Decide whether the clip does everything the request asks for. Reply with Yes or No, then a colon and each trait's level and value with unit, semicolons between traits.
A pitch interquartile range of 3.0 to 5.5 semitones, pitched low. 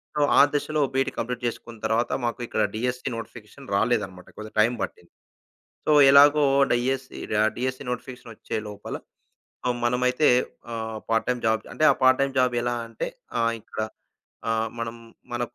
No: narrow, 2.4 semitones; low, 120 Hz